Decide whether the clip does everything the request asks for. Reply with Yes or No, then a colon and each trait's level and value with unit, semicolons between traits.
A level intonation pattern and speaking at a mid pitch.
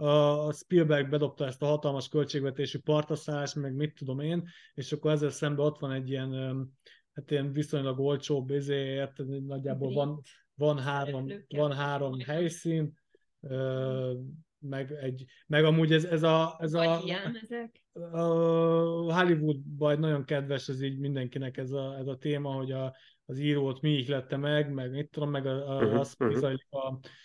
Yes: narrow, 1.9 semitones; medium, 145 Hz